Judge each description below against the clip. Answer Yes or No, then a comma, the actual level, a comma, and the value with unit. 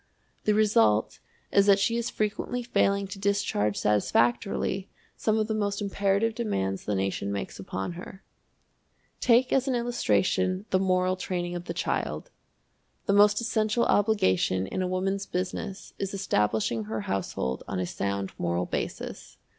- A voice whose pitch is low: No, high, 190 Hz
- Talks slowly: No, average, 150 wpm